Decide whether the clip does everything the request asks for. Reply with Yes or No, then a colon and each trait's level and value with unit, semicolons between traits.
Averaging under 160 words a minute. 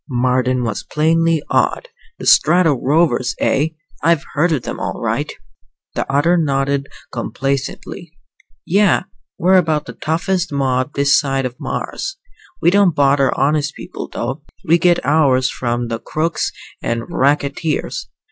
Yes: average, 140 wpm